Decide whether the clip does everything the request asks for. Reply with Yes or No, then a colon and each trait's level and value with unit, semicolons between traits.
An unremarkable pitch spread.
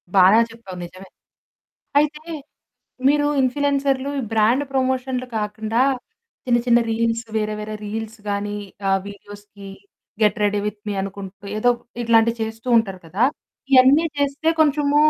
Yes: average, 4.2 semitones